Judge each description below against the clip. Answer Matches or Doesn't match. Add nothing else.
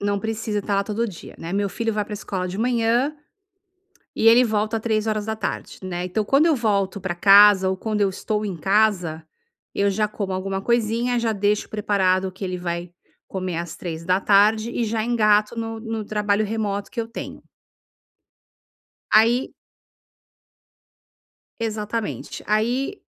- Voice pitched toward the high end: Matches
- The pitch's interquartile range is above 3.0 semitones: Doesn't match